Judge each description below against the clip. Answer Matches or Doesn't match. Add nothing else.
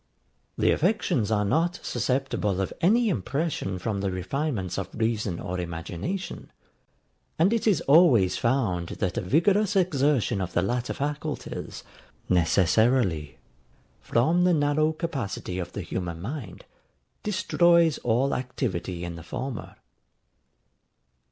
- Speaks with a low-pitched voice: Matches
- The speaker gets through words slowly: Matches